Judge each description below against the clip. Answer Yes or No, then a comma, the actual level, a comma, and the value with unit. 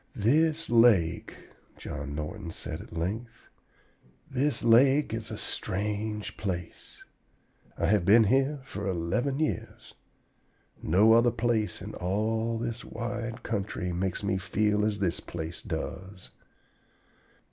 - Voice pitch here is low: Yes, low, 105 Hz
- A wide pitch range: No, average, 4.1 semitones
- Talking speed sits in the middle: No, slow, 120 wpm